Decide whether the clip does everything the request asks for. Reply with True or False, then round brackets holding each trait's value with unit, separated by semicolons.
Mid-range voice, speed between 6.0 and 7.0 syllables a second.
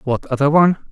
True (145 Hz; 6.9 syllables/s)